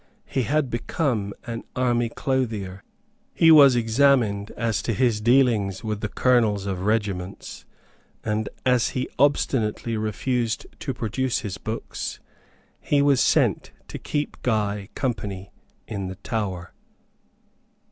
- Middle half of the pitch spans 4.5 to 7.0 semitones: No, average, 3.8 semitones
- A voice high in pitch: No, low, 115 Hz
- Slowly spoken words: Yes, slow, 125 wpm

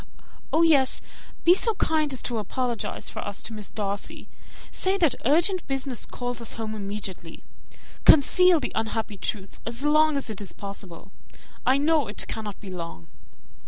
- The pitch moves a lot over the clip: Yes, wide, 6.8 semitones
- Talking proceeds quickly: No, average, 160 wpm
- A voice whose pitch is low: No, high, 240 Hz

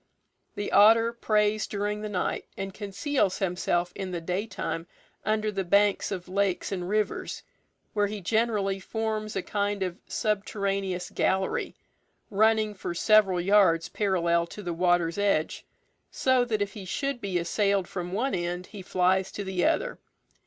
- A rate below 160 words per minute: Yes, average, 150 wpm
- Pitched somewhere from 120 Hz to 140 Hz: No, high, 200 Hz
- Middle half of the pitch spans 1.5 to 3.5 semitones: Yes, average, 2.7 semitones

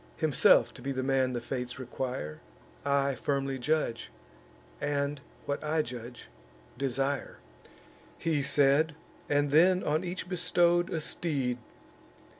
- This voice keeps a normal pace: No, slow, 120 wpm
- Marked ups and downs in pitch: No, average, 3.3 semitones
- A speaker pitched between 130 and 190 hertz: Yes, medium, 140 Hz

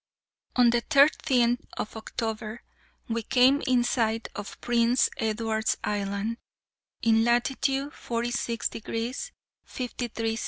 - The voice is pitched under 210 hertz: No, high, 235 Hz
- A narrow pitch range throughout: Yes, narrow, 1.8 semitones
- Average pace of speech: No, slow, 110 wpm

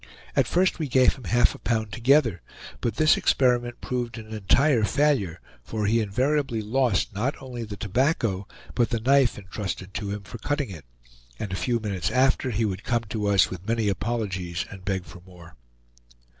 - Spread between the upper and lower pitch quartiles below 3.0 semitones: No, average, 4.3 semitones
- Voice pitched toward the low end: Yes, low, 110 Hz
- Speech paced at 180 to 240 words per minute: Yes, average, 185 wpm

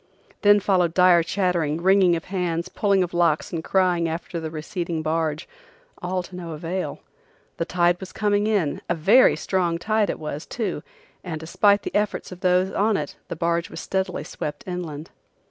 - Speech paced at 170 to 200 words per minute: Yes, average, 180 wpm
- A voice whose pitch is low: No, medium, 175 Hz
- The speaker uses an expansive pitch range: No, narrow, 2.5 semitones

